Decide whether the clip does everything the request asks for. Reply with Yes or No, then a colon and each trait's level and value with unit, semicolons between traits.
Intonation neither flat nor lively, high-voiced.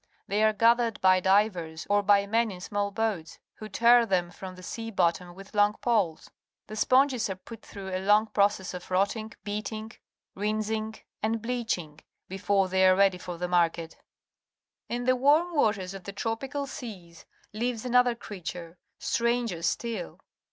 Yes: average, 3.6 semitones; high, 205 Hz